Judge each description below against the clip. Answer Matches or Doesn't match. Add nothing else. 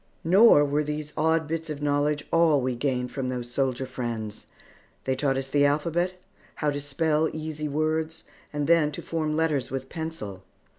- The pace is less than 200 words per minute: Matches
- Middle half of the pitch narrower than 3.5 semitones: Matches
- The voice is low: Doesn't match